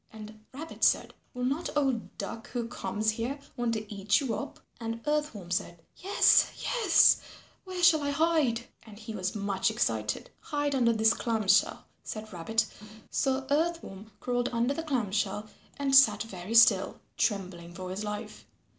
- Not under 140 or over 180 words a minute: Yes, average, 170 wpm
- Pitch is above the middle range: Yes, high, 230 Hz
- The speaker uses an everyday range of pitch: Yes, average, 5.0 semitones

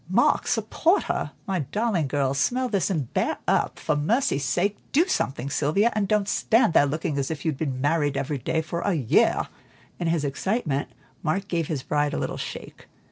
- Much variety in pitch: Yes, wide, 5.8 semitones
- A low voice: No, medium, 160 Hz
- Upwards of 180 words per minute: Yes, average, 190 wpm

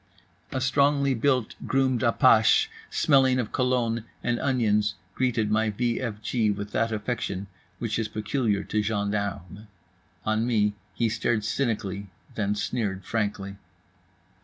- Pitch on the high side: No, low, 110 Hz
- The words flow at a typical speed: No, slow, 130 wpm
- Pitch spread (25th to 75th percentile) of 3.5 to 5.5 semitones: No, average, 3.1 semitones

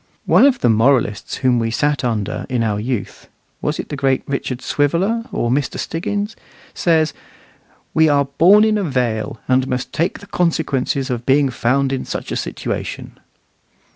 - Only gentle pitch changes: No, average, 4.6 semitones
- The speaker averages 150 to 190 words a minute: Yes, average, 170 wpm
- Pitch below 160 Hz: Yes, low, 135 Hz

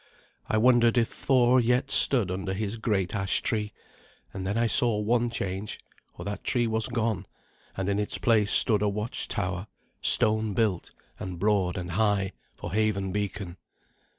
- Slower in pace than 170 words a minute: Yes, average, 160 wpm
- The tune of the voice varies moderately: Yes, average, 3.0 semitones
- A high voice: No, low, 105 Hz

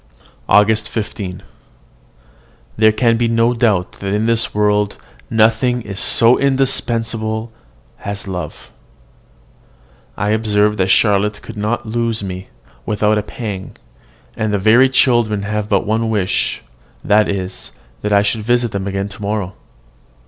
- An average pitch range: No, narrow, 2.1 semitones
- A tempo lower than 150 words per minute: Yes, slow, 135 wpm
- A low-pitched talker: Yes, low, 105 Hz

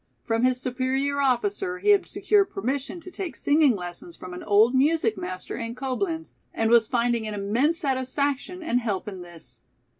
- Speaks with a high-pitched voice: Yes, very high, 255 Hz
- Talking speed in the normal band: Yes, average, 175 wpm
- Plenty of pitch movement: Yes, wide, 6.4 semitones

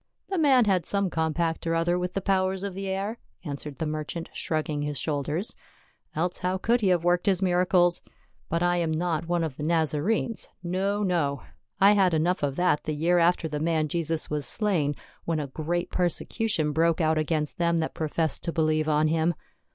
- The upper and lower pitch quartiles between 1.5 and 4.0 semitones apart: Yes, average, 2.8 semitones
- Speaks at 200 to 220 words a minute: Yes, fast, 205 wpm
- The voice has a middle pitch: Yes, medium, 170 Hz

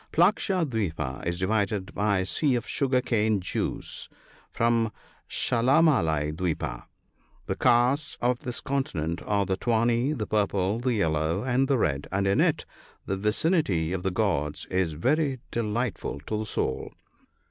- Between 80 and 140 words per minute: No, average, 155 wpm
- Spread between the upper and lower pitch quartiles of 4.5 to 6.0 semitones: Yes, average, 5.3 semitones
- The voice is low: Yes, low, 105 Hz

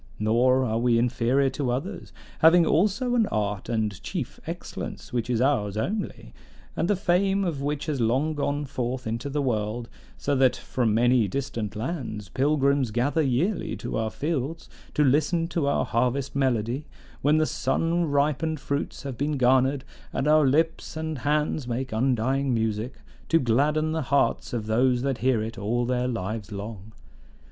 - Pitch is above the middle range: No, low, 130 Hz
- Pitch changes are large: No, average, 4.3 semitones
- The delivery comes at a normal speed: Yes, average, 165 wpm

